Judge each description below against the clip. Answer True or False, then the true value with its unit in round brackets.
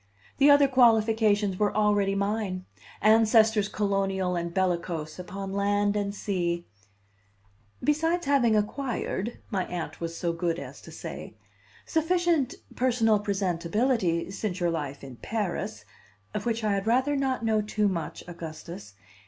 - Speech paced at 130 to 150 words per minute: True (135 wpm)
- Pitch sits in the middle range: False (205 Hz)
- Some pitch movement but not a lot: True (4.4 semitones)